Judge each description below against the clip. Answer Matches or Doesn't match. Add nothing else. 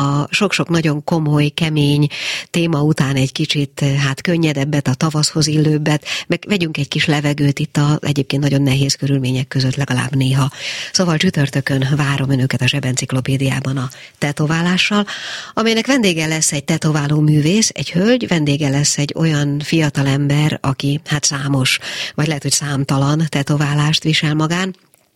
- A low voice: Doesn't match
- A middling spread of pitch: Doesn't match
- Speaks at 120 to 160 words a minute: Matches